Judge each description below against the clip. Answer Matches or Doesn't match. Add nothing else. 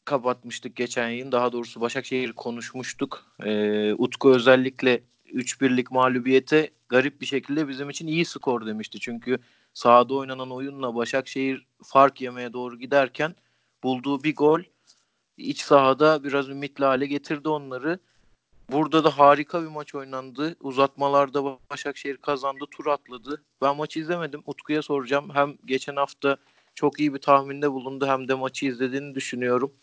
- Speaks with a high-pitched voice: Doesn't match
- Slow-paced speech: Doesn't match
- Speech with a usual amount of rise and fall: Doesn't match